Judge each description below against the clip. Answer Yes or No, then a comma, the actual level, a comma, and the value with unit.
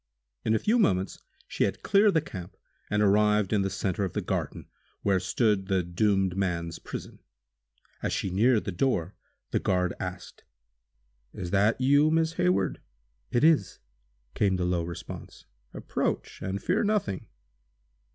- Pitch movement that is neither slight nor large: Yes, average, 4.7 semitones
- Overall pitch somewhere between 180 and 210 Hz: No, low, 100 Hz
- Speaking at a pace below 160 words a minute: Yes, average, 150 wpm